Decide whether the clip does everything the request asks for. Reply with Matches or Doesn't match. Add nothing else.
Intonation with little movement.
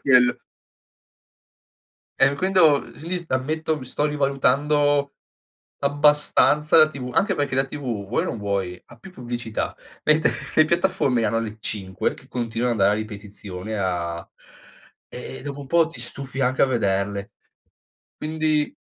Doesn't match